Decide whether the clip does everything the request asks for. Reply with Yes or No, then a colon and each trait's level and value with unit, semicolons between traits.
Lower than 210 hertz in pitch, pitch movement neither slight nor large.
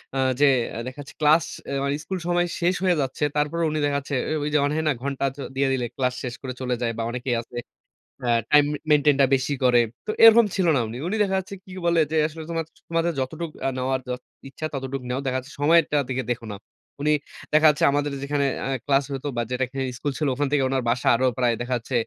Yes: medium, 140 Hz; average, 3.2 semitones